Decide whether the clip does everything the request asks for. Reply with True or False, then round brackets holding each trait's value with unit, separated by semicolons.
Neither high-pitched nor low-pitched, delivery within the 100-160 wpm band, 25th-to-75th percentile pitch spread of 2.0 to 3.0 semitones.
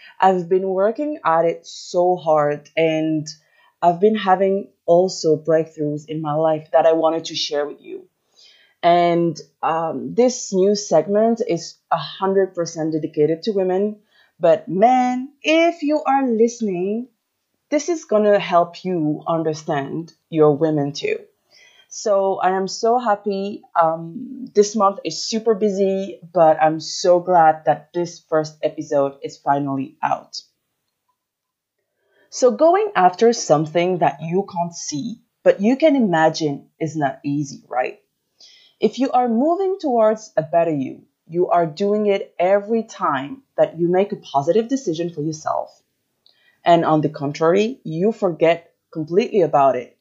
False (180 Hz; 140 wpm; 5.5 semitones)